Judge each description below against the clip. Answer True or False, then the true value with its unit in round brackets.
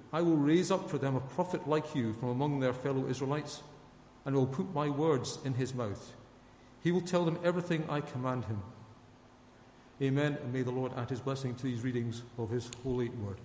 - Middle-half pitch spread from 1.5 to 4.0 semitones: True (2.9 semitones)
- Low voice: True (130 Hz)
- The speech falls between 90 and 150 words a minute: False (205 wpm)